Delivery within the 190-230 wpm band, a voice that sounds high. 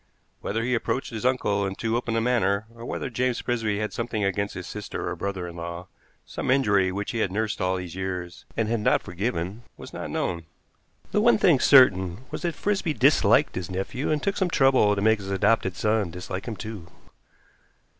No: fast, 205 wpm; low, 105 Hz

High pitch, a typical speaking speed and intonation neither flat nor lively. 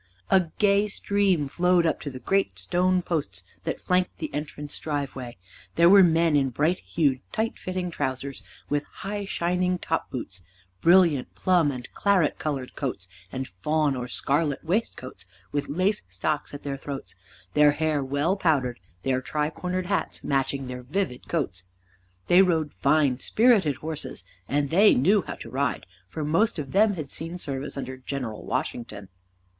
No: medium, 150 Hz; average, 160 wpm; average, 5.0 semitones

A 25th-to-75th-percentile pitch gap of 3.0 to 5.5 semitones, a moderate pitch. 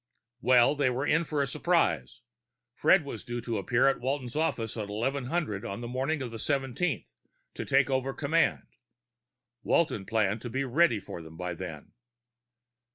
No: average, 4.3 semitones; low, 125 Hz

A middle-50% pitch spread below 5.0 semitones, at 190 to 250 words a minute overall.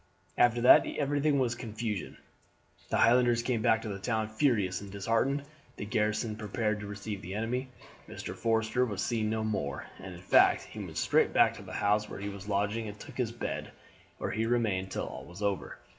Yes: average, 2.7 semitones; average, 200 wpm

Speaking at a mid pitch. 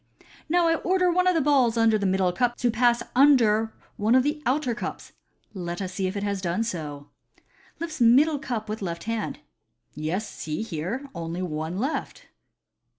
No: high, 225 Hz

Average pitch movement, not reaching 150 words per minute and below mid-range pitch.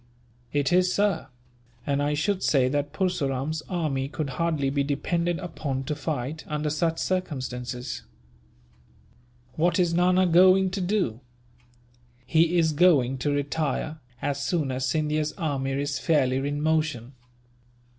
No: average, 3.8 semitones; slow, 135 wpm; medium, 150 Hz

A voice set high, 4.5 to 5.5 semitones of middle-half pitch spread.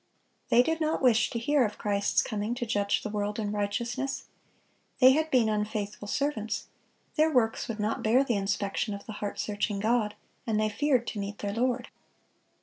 No: high, 220 Hz; average, 3.2 semitones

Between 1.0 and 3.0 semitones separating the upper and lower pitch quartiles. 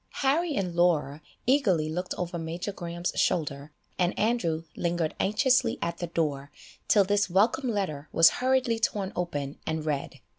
No: average, 4.9 semitones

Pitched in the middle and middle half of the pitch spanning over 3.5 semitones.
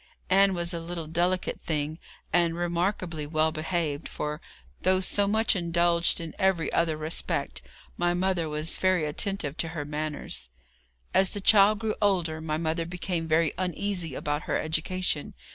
No: medium, 170 Hz; average, 2.9 semitones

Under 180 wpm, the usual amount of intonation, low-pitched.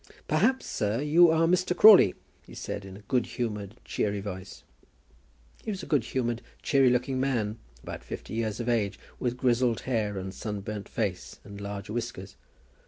Yes: average, 170 wpm; average, 4.6 semitones; low, 115 Hz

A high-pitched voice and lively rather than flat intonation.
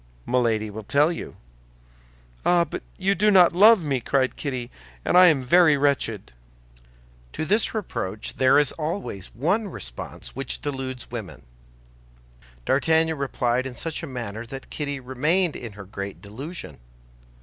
No: low, 135 Hz; wide, 5.7 semitones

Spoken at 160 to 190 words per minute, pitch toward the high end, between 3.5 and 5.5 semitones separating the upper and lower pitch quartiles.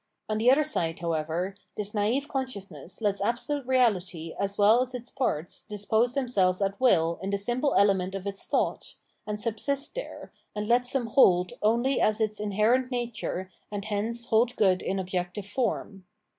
Yes: average, 170 wpm; high, 210 Hz; average, 4.2 semitones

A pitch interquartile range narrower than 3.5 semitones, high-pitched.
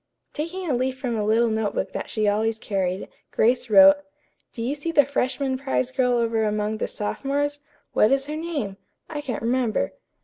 No: average, 4.6 semitones; high, 245 Hz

